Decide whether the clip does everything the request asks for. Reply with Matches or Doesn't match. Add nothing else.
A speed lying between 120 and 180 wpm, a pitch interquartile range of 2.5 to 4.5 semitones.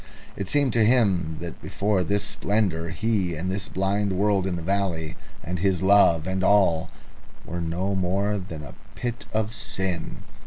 Matches